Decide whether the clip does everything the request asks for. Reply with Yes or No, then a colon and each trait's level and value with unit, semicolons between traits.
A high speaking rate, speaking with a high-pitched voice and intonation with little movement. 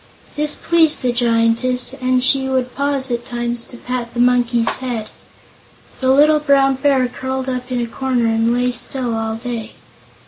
No: average, 170 wpm; very high, 250 Hz; narrow, 1.8 semitones